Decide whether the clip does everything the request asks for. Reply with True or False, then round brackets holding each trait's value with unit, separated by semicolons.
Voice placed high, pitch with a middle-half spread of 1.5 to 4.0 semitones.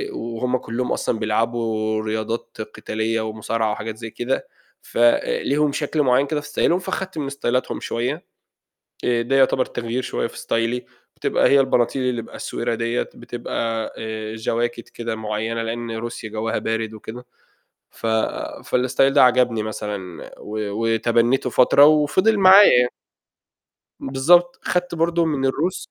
False (120 Hz; 3.3 semitones)